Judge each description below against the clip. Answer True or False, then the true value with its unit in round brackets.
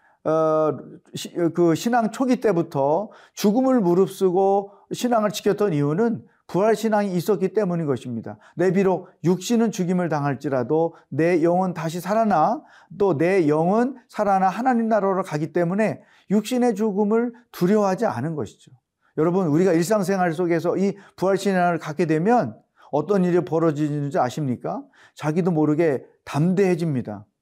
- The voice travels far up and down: False (4.8 semitones)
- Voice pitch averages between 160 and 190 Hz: True (185 Hz)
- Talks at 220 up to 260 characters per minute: False (315 characters per minute)